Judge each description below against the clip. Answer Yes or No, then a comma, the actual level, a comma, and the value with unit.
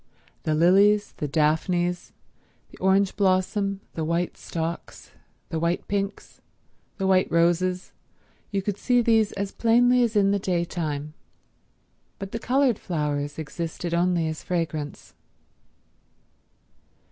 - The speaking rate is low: Yes, slow, 120 wpm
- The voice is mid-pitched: Yes, medium, 180 Hz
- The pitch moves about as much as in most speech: Yes, average, 3.4 semitones